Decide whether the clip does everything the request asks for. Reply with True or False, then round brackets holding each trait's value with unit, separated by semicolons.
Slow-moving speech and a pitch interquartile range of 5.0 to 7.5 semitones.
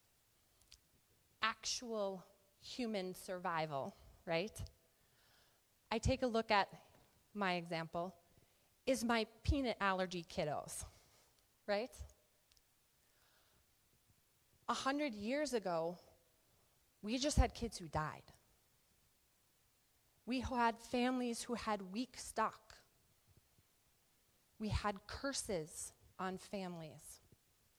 True (85 wpm; 5.5 semitones)